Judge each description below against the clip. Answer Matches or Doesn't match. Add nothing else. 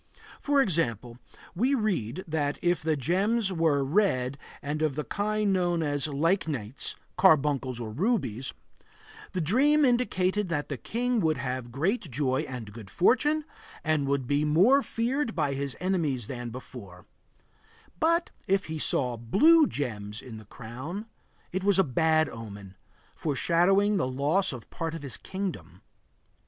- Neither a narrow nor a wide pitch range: Doesn't match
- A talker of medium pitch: Matches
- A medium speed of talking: Matches